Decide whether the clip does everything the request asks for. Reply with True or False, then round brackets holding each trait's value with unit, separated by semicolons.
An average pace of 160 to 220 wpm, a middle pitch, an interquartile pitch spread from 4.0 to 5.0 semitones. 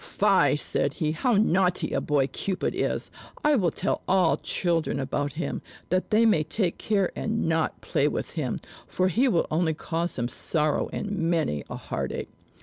True (175 wpm; 170 Hz; 4.3 semitones)